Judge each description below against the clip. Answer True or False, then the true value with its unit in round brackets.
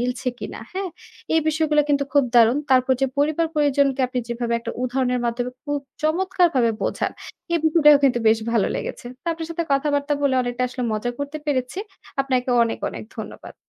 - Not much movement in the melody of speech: False (3.4 semitones)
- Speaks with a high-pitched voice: True (275 Hz)